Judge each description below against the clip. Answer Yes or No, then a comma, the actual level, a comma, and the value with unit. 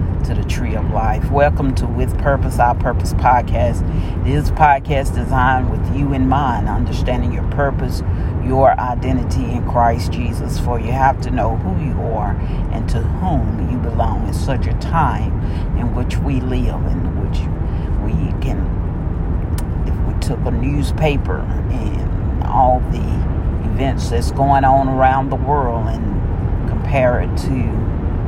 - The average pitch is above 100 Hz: No, very low, 90 Hz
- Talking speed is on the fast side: No, average, 155 wpm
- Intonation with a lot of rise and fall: Yes, wide, 6.4 semitones